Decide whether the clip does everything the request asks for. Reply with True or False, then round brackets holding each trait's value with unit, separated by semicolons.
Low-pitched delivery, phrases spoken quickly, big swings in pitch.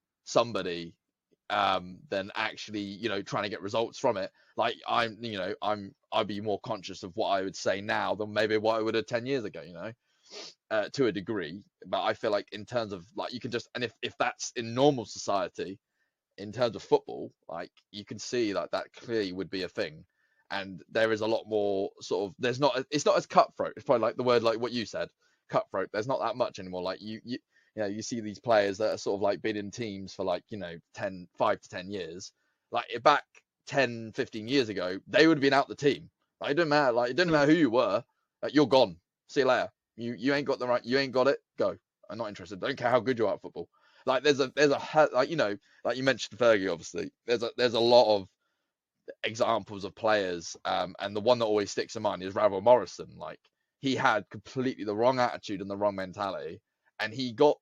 False (115 Hz; 240 wpm; 4.7 semitones)